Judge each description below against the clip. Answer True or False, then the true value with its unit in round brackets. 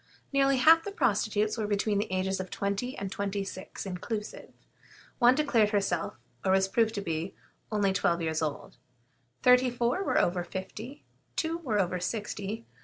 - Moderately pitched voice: False (205 Hz)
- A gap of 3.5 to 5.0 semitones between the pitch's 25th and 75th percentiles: True (4.2 semitones)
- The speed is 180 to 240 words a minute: False (165 wpm)